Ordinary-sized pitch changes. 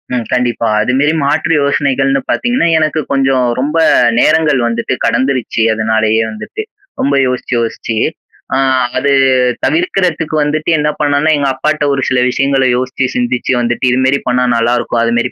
Yes: average, 3.4 semitones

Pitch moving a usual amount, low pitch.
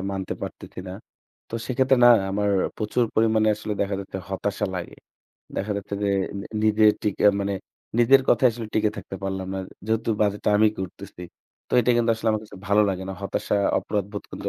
No: narrow, 2.2 semitones; low, 105 Hz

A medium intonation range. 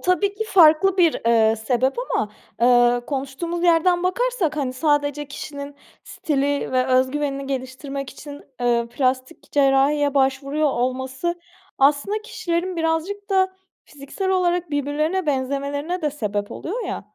Yes: average, 4.6 semitones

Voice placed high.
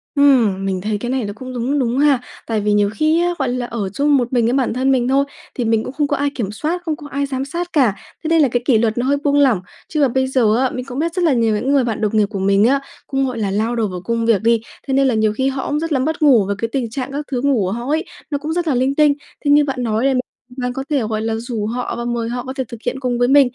Yes: very high, 255 Hz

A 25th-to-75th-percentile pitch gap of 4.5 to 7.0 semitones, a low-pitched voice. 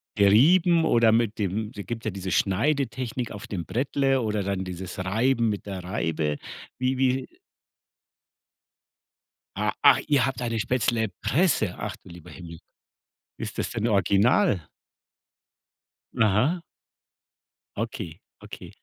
Yes: average, 4.9 semitones; low, 110 Hz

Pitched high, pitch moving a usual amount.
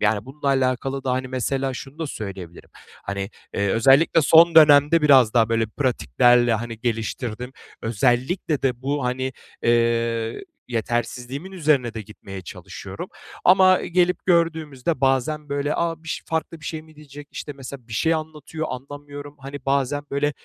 No: low, 135 Hz; average, 4.2 semitones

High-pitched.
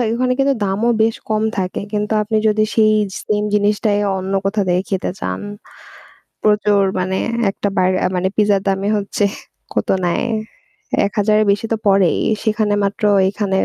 Yes: high, 205 Hz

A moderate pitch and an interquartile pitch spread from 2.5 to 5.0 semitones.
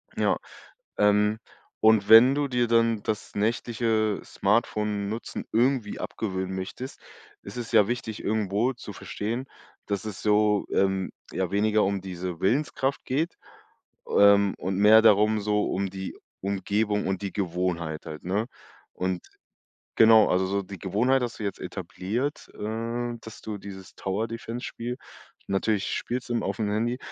No: low, 105 Hz; average, 2.9 semitones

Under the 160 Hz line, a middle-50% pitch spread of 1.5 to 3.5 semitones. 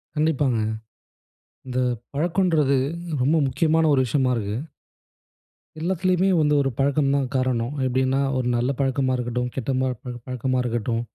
Yes: low, 135 Hz; average, 3.2 semitones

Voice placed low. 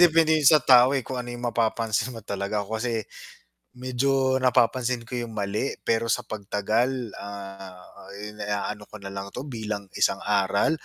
Yes: low, 115 Hz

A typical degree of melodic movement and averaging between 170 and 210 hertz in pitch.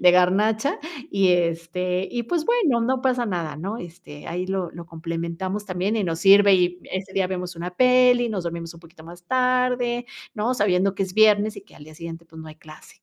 Yes: average, 4.5 semitones; medium, 185 Hz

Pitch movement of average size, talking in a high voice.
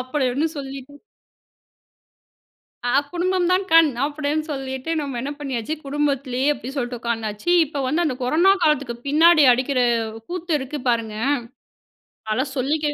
Yes: average, 3.3 semitones; very high, 280 Hz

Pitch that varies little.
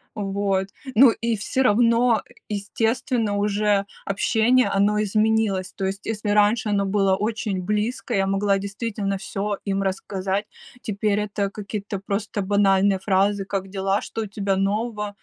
Yes: narrow, 1.6 semitones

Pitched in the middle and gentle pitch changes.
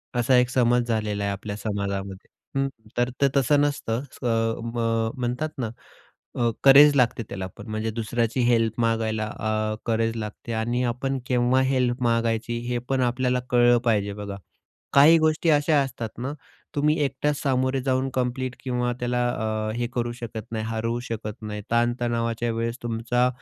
No: low, 120 Hz; narrow, 2.3 semitones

